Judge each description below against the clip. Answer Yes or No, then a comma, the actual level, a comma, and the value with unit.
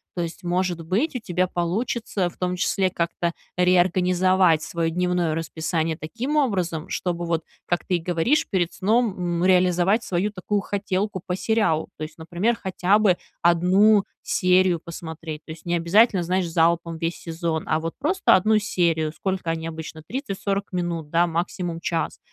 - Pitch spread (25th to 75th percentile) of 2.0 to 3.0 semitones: Yes, narrow, 2.5 semitones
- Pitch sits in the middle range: Yes, medium, 180 Hz